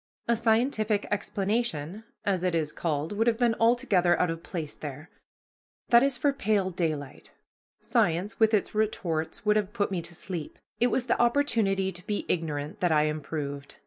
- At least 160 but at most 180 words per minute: Yes, average, 175 wpm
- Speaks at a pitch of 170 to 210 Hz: Yes, high, 190 Hz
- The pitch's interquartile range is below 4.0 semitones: No, wide, 5.4 semitones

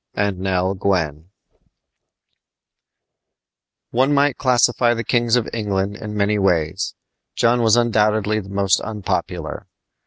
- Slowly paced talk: Yes, slow, 115 wpm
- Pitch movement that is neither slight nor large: Yes, average, 3.5 semitones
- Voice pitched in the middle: No, low, 105 Hz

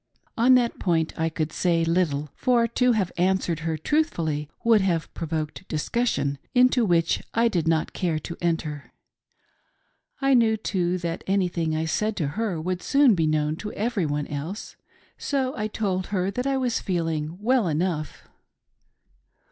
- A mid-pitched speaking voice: Yes, medium, 180 Hz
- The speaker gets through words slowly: No, average, 155 wpm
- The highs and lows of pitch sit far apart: Yes, wide, 5.7 semitones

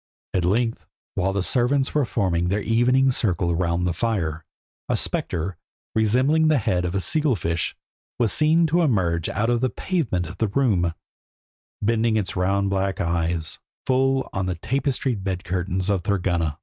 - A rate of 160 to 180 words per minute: Yes, average, 165 wpm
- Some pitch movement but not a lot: No, wide, 6.0 semitones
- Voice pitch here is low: Yes, low, 100 Hz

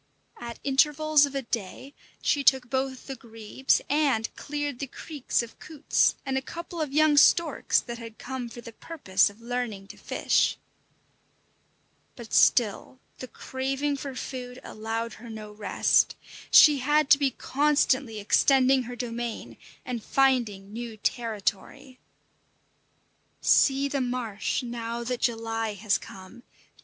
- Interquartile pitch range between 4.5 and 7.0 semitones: No, average, 3.3 semitones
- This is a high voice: Yes, very high, 250 Hz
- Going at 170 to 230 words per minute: No, average, 140 wpm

